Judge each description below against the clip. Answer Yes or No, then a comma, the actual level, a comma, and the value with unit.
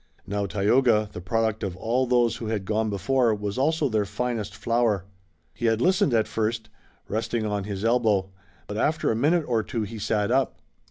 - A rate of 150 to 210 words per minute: Yes, average, 185 wpm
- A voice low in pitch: Yes, low, 110 Hz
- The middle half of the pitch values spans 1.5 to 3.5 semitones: Yes, average, 2.8 semitones